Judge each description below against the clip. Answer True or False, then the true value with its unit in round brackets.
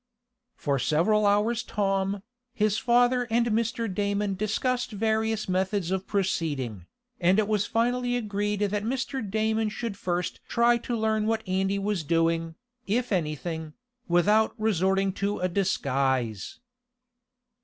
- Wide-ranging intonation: False (3.3 semitones)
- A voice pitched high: True (205 Hz)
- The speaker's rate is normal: False (130 wpm)